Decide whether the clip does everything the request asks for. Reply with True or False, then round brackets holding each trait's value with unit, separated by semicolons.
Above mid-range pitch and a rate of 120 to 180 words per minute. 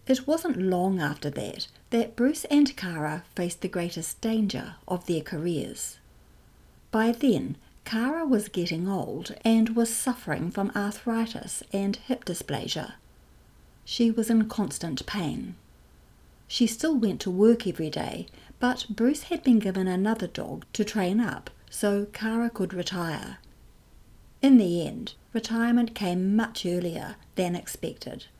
True (210 Hz; 135 wpm)